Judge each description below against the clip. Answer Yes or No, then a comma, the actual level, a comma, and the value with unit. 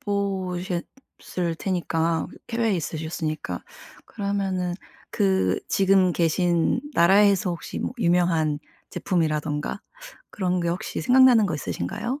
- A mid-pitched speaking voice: Yes, medium, 180 Hz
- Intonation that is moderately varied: Yes, average, 3.3 semitones